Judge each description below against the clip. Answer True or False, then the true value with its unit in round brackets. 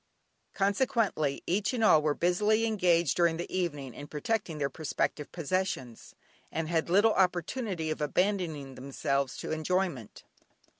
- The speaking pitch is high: False (170 Hz)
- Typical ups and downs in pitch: True (4.7 semitones)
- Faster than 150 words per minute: False (135 wpm)